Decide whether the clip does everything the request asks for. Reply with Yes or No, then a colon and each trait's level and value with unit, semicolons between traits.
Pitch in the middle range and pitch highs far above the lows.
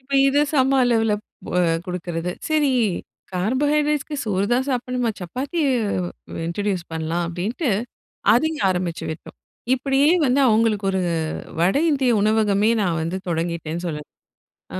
No: high, 215 Hz; wide, 7.0 semitones